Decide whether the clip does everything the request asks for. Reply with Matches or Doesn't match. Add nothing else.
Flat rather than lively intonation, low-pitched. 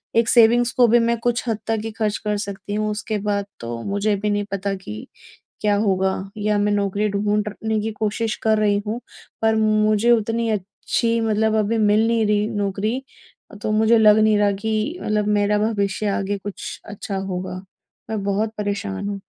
Doesn't match